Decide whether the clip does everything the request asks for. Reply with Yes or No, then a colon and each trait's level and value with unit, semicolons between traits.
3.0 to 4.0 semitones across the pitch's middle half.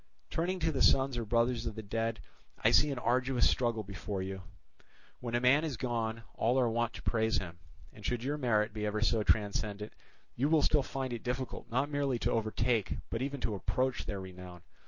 Yes: average, 3.4 semitones